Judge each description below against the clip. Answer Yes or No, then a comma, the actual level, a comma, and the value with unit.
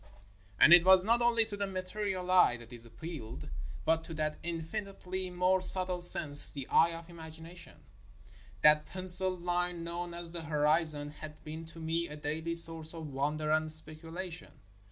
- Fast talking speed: No, average, 170 wpm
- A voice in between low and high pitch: Yes, medium, 165 Hz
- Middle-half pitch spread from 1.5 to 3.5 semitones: Yes, average, 2.7 semitones